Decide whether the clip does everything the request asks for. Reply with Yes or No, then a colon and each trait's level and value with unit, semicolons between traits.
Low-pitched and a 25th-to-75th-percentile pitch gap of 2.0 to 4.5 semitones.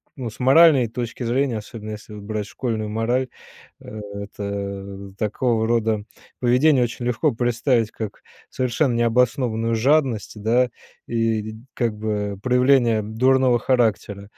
Yes: low, 115 Hz; average, 2.8 semitones